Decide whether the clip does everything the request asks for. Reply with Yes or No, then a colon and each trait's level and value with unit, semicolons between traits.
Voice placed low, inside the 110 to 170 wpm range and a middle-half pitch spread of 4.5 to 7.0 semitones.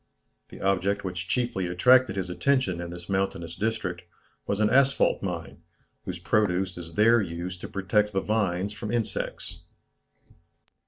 No: very low, 95 Hz; average, 145 wpm; average, 3.3 semitones